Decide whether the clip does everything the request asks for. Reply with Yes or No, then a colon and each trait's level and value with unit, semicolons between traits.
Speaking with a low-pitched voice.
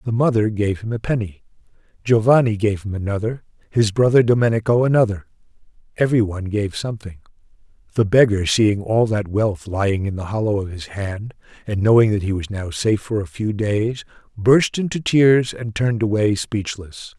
Yes: low, 105 Hz